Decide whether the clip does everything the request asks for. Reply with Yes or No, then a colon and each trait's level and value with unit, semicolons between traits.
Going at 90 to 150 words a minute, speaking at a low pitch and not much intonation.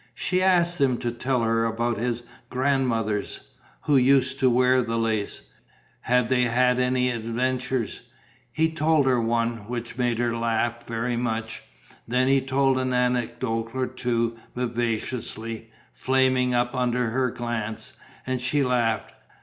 Yes: average, 140 wpm; low, 125 Hz; narrow, 1.9 semitones